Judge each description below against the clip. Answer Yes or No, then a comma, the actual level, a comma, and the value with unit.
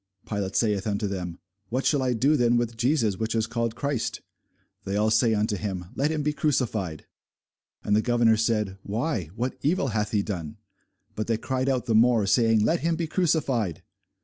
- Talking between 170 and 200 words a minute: Yes, average, 190 wpm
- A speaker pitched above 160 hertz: No, low, 115 Hz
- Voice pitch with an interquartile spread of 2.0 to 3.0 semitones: No, average, 3.8 semitones